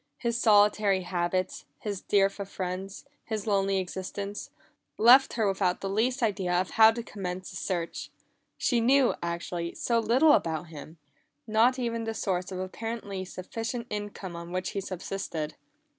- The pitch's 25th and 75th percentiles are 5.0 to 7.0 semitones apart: No, average, 3.5 semitones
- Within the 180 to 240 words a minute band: No, average, 160 wpm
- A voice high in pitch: Yes, high, 195 Hz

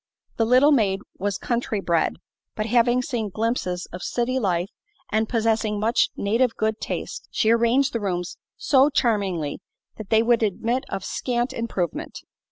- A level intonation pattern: No, average, 3.2 semitones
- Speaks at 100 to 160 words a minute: Yes, average, 155 wpm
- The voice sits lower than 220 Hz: No, high, 225 Hz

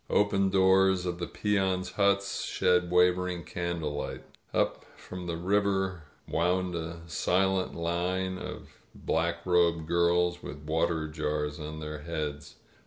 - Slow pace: Yes, slow, 125 wpm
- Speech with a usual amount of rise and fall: No, narrow, 2.2 semitones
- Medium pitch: No, very low, 90 Hz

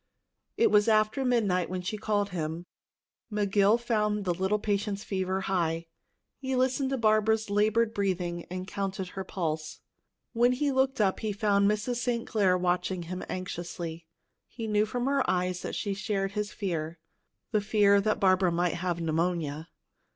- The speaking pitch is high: Yes, high, 200 Hz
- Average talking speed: Yes, average, 160 wpm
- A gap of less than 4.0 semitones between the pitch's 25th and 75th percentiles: Yes, average, 3.2 semitones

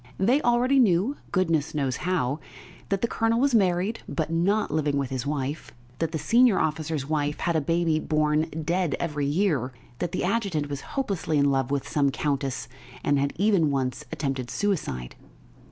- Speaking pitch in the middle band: Yes, medium, 155 Hz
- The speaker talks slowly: No, average, 170 wpm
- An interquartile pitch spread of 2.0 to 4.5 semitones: No, average, 5.2 semitones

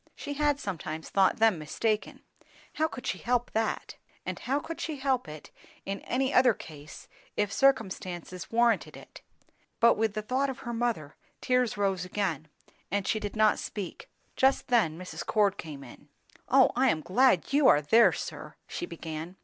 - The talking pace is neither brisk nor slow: Yes, average, 175 wpm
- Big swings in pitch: Yes, wide, 5.9 semitones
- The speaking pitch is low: No, high, 215 Hz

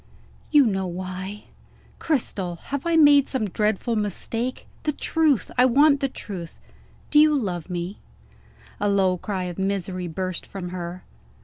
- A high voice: Yes, high, 200 Hz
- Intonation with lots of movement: Yes, wide, 6.7 semitones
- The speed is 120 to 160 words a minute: Yes, average, 145 wpm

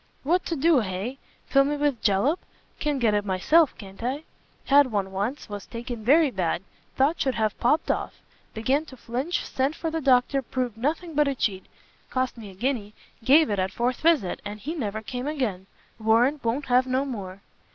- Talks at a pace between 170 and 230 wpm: Yes, average, 195 wpm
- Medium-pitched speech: No, very high, 250 Hz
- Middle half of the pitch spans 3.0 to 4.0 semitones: No, average, 5.2 semitones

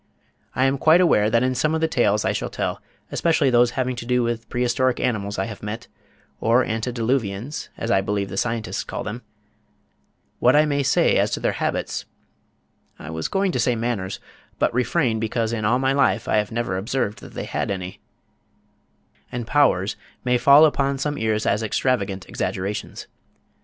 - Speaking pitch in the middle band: No, low, 120 Hz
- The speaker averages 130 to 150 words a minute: No, average, 185 wpm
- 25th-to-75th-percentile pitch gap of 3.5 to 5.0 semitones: Yes, average, 3.8 semitones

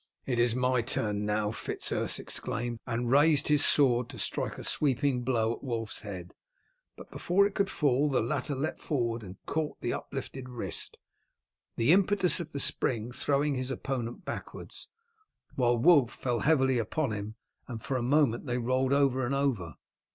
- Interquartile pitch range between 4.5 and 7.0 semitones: No, average, 3.4 semitones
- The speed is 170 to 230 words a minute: Yes, average, 175 wpm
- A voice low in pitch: Yes, low, 130 Hz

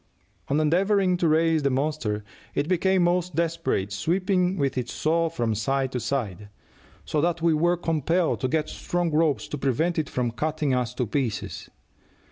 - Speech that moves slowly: No, average, 170 wpm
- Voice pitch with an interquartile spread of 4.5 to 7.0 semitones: Yes, average, 4.8 semitones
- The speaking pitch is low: No, medium, 155 Hz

